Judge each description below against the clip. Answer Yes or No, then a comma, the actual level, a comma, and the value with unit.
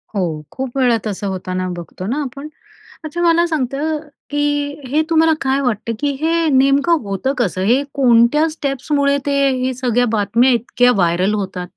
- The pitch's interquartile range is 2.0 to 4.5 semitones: No, average, 5.3 semitones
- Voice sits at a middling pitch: No, very high, 255 Hz